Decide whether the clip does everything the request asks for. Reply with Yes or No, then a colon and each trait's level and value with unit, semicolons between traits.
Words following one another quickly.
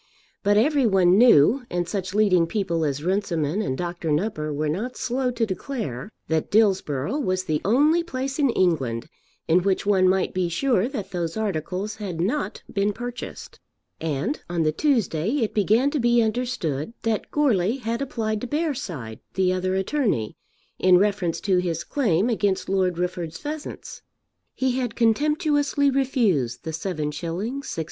No: average, 155 wpm